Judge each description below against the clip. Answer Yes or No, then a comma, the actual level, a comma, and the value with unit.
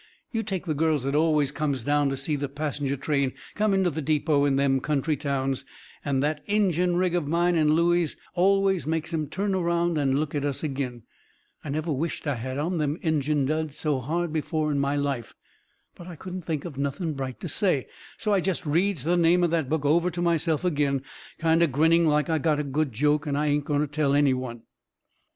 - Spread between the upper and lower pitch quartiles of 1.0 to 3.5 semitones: Yes, average, 3.2 semitones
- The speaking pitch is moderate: Yes, medium, 150 Hz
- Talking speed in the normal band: No, fast, 220 wpm